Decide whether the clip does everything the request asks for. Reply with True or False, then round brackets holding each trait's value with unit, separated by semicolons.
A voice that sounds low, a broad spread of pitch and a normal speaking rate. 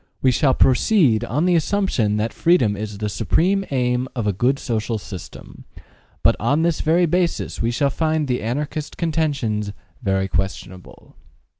True (125 Hz; 6.8 semitones; 155 wpm)